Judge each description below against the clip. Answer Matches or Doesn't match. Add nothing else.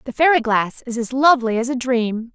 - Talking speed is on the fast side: Matches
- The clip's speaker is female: Matches